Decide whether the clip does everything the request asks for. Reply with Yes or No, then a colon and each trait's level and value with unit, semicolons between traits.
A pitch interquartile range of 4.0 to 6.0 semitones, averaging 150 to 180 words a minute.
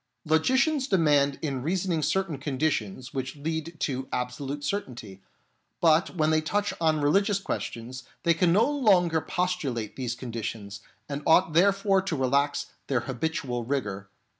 No: wide, 5.5 semitones; average, 140 wpm